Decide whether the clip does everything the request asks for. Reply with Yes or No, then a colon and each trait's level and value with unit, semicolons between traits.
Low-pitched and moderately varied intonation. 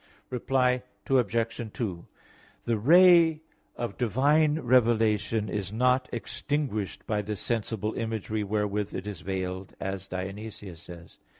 Yes: low, 110 Hz; average, 4.1 semitones